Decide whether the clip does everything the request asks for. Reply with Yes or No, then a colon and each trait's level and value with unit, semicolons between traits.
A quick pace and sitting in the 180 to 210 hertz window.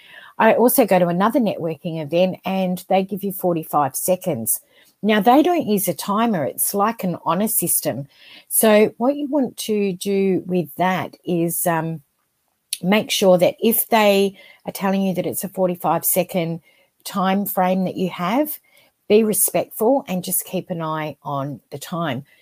No: average, 165 wpm; medium, 185 Hz